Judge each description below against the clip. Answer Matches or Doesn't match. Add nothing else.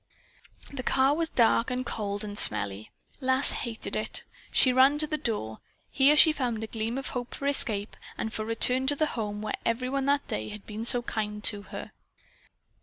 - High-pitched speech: Matches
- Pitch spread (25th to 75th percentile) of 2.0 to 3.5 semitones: Doesn't match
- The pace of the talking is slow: Doesn't match